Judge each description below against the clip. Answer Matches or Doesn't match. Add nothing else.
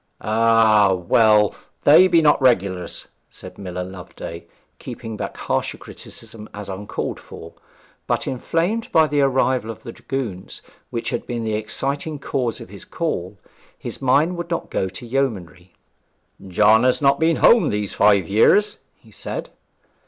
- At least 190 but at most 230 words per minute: Doesn't match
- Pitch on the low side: Matches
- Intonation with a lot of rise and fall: Matches